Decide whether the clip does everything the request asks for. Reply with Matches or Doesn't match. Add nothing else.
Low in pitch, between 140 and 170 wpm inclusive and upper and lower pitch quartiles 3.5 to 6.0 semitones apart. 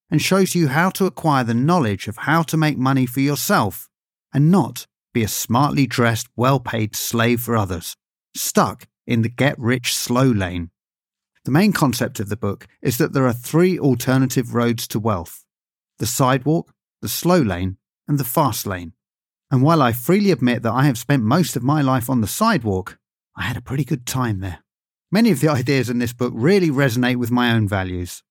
Doesn't match